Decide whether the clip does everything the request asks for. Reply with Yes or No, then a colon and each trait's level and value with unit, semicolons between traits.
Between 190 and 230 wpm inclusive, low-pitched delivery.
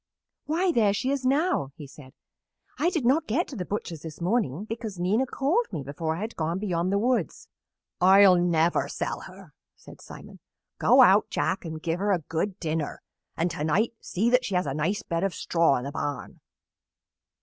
No: average, 195 wpm; medium, 185 Hz